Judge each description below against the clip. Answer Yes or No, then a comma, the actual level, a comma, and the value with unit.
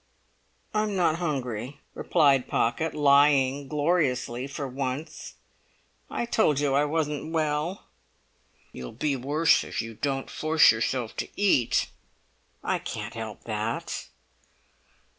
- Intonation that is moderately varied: Yes, average, 3.7 semitones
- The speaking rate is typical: No, slow, 115 wpm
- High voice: No, medium, 140 Hz